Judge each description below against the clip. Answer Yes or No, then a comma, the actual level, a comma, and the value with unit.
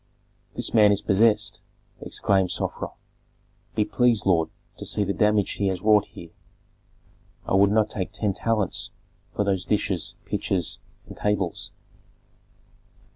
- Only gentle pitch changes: Yes, narrow, 1.8 semitones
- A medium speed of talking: No, slow, 130 wpm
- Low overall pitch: Yes, low, 100 Hz